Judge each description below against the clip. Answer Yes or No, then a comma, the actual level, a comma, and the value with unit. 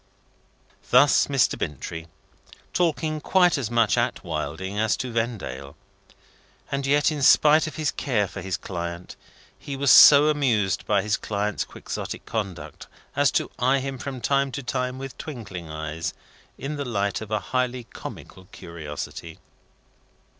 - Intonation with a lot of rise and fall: Yes, wide, 6.5 semitones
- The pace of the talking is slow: No, average, 145 wpm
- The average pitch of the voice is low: Yes, low, 120 Hz